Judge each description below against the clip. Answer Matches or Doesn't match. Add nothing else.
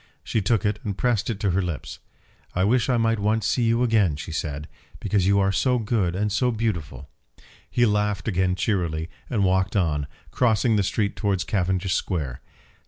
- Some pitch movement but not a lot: Matches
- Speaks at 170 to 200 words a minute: Matches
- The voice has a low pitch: Matches